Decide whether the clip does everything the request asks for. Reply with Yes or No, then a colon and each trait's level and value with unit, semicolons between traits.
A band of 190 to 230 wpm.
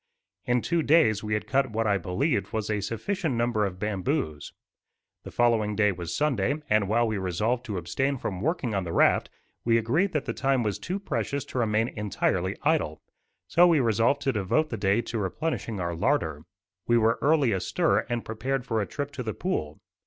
Yes: average, 195 wpm